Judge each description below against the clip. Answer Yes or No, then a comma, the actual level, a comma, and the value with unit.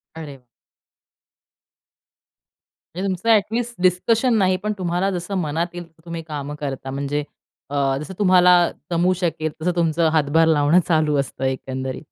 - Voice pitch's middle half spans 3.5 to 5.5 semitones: Yes, average, 3.8 semitones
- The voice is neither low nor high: Yes, medium, 170 Hz